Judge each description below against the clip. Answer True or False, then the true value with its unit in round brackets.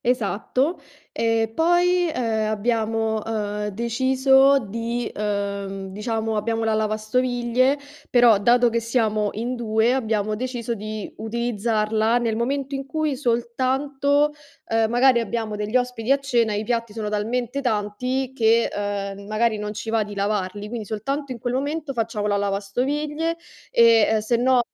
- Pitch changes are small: False (3.1 semitones)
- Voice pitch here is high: True (230 Hz)